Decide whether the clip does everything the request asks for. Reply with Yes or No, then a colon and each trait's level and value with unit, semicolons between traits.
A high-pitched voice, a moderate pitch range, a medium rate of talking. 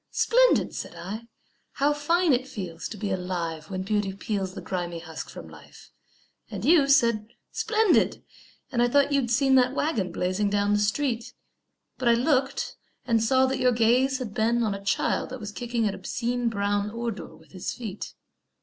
Yes: high, 230 Hz; average, 4.7 semitones; average, 180 wpm